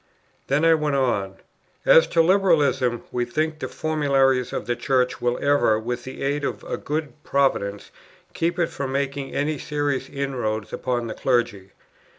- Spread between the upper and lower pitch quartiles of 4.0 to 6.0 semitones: No, average, 3.6 semitones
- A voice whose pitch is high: No, low, 135 Hz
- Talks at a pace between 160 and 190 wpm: Yes, average, 165 wpm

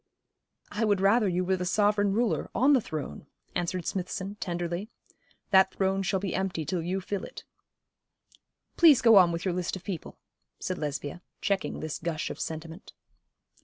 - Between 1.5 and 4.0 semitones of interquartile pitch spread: Yes, average, 2.8 semitones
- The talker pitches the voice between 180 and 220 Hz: Yes, medium, 185 Hz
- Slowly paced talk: No, average, 165 wpm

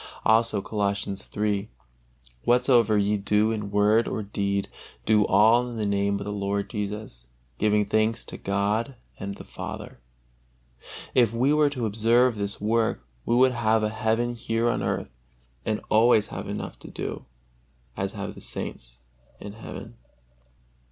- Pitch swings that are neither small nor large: No, narrow, 2.3 semitones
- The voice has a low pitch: Yes, low, 110 Hz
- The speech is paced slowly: No, average, 150 wpm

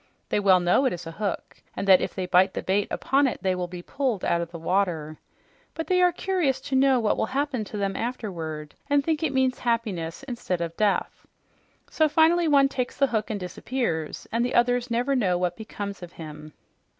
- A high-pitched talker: Yes, high, 215 Hz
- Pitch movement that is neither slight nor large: No, wide, 6.9 semitones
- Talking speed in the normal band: No, fast, 215 wpm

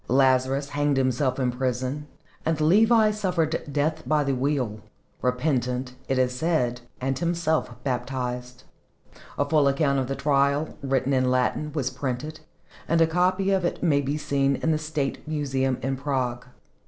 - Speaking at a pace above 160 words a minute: No, average, 155 wpm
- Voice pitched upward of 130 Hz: Yes, medium, 140 Hz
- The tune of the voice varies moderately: Yes, average, 3.2 semitones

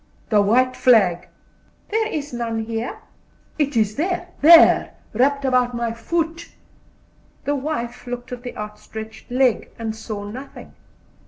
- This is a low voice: No, high, 245 Hz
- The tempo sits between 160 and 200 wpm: No, slow, 135 wpm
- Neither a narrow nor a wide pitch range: Yes, average, 4.2 semitones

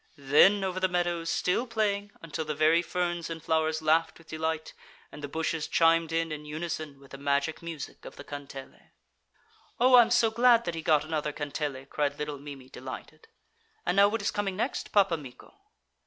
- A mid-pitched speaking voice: Yes, medium, 160 Hz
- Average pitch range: Yes, average, 3.6 semitones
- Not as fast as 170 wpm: No, average, 185 wpm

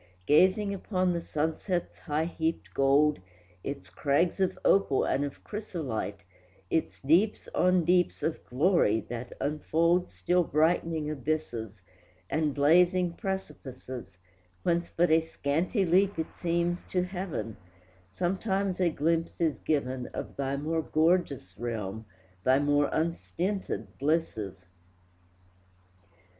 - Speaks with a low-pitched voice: No, medium, 160 Hz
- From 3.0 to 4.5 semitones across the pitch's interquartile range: Yes, average, 4.2 semitones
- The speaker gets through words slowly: Yes, slow, 115 wpm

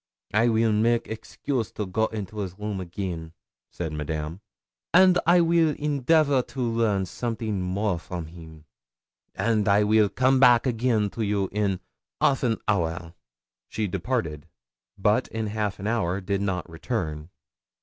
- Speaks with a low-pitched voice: Yes, low, 105 Hz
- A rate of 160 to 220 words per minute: No, average, 150 wpm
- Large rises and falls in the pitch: No, average, 4.4 semitones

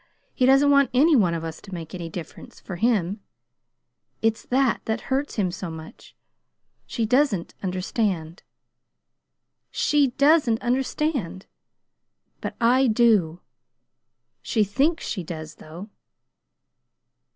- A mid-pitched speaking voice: No, high, 220 Hz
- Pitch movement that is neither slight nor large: No, wide, 7.0 semitones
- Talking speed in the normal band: No, slow, 115 wpm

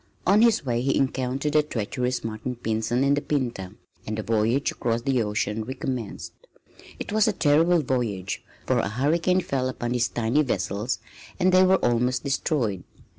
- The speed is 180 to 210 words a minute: No, average, 170 wpm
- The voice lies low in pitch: Yes, low, 125 Hz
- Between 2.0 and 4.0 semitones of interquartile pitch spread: No, average, 4.4 semitones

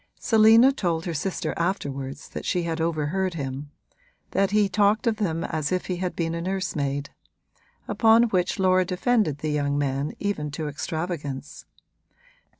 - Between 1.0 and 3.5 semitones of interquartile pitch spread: No, average, 4.8 semitones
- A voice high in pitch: No, medium, 170 Hz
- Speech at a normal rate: Yes, average, 150 wpm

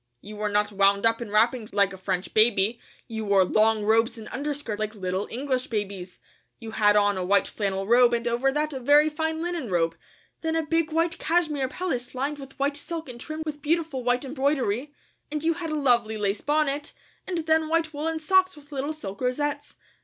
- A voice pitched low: No, very high, 255 Hz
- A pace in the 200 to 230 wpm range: Yes, fast, 205 wpm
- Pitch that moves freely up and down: Yes, wide, 6.3 semitones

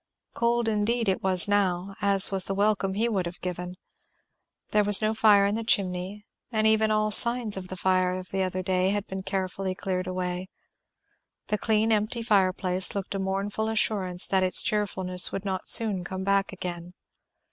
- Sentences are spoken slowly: No, average, 185 wpm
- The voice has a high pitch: Yes, high, 195 Hz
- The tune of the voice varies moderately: No, narrow, 2.3 semitones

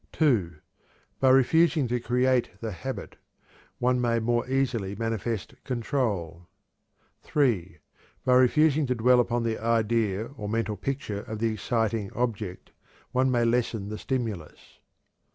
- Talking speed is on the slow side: Yes, slow, 130 wpm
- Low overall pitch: Yes, low, 115 Hz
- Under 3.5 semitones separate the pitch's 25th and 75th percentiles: Yes, average, 3.0 semitones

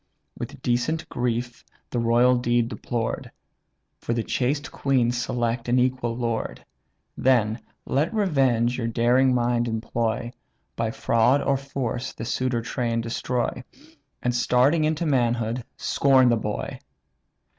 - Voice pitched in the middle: No, low, 120 Hz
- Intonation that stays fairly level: Yes, narrow, 1.8 semitones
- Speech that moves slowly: Yes, slow, 125 wpm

